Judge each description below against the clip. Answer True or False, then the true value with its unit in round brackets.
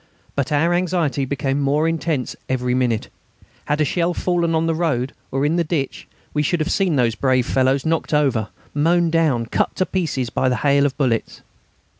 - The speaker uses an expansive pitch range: False (4.0 semitones)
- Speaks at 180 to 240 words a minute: True (190 wpm)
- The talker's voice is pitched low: False (145 Hz)